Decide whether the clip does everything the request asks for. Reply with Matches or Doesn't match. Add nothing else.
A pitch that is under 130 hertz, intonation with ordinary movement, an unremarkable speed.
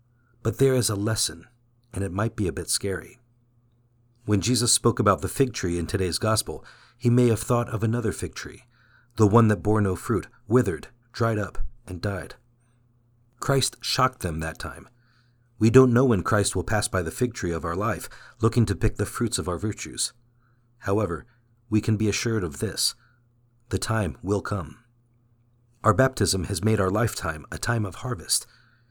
Matches